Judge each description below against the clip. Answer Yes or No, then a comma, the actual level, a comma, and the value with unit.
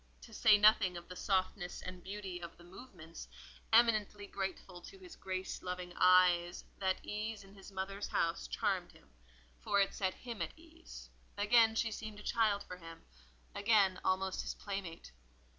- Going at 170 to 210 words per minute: No, average, 160 wpm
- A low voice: No, high, 195 Hz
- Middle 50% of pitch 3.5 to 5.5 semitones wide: No, average, 2.7 semitones